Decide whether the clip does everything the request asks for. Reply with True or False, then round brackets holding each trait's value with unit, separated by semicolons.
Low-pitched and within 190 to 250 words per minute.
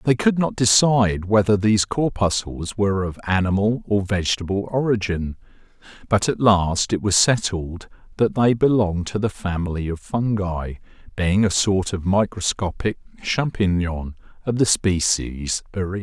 False (100 Hz; 140 wpm)